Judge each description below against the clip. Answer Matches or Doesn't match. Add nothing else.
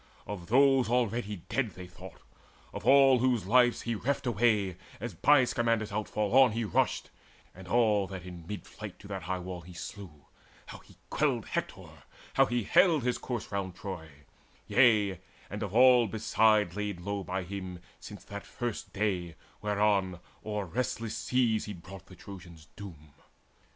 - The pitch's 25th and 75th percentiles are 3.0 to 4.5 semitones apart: Matches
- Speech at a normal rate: Matches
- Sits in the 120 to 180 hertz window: Doesn't match